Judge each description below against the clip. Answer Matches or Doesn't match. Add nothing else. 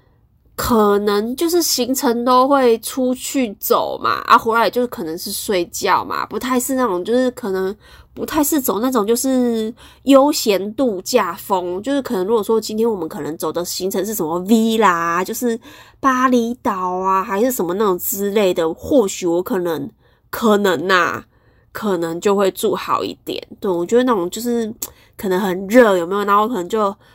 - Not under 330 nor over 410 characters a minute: Doesn't match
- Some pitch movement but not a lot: Matches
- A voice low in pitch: Doesn't match